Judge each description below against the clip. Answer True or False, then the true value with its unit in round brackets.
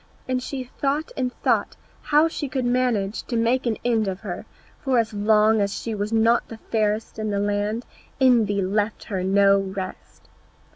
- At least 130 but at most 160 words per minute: False (180 wpm)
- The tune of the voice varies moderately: True (3.5 semitones)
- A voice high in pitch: True (220 Hz)